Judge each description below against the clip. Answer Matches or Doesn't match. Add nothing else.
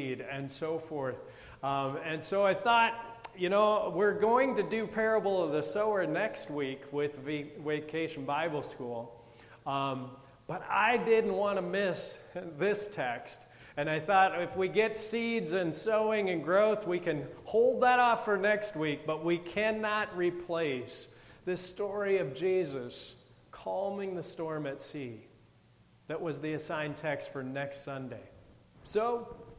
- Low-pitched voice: Doesn't match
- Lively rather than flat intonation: Matches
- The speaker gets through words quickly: Doesn't match